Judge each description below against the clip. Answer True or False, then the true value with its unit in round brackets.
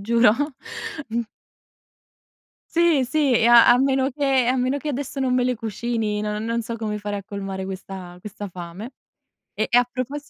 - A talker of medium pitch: False (235 Hz)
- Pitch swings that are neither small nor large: True (4.0 semitones)